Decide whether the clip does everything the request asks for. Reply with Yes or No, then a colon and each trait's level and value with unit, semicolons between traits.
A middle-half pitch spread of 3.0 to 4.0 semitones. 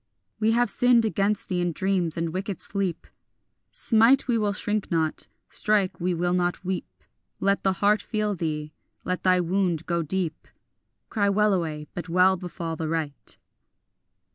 Yes: average, 3.4 semitones